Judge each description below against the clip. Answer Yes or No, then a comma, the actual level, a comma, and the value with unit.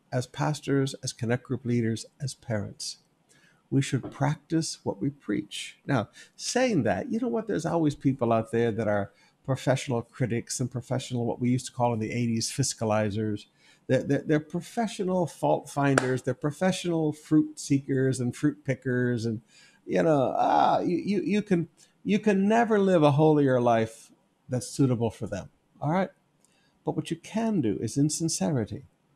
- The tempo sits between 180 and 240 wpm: No, average, 170 wpm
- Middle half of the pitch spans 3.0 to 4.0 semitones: No, wide, 5.4 semitones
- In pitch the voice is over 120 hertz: Yes, medium, 140 Hz